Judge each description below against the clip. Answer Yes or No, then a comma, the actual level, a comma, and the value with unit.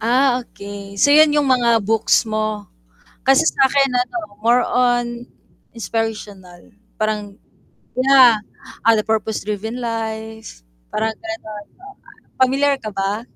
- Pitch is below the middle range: No, high, 225 Hz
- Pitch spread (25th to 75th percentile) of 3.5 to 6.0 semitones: No, average, 3.1 semitones